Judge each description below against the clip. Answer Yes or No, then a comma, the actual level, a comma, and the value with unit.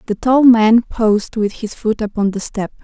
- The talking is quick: Yes, fast, 210 wpm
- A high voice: Yes, high, 220 Hz